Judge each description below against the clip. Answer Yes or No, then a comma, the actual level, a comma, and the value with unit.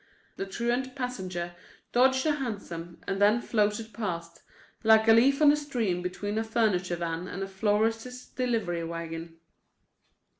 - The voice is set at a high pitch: Yes, high, 210 Hz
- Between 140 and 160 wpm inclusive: Yes, average, 145 wpm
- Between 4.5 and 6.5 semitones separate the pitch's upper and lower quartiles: Yes, average, 5.3 semitones